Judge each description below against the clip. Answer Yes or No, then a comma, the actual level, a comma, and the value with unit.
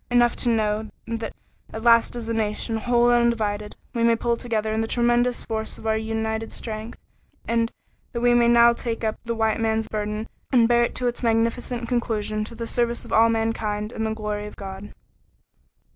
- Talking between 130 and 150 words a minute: No, average, 200 wpm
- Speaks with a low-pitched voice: No, high, 225 Hz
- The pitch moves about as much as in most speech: No, narrow, 1.4 semitones